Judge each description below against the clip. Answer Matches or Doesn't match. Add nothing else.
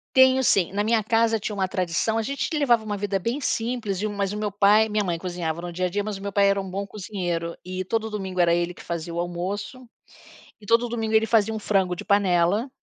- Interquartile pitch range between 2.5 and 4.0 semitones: Matches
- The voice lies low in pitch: Doesn't match